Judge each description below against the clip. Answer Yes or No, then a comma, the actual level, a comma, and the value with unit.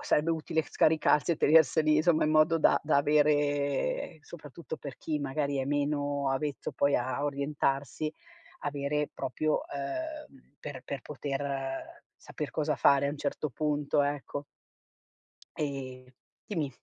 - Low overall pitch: No, medium, 145 Hz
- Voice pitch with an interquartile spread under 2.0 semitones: Yes, narrow, 1.6 semitones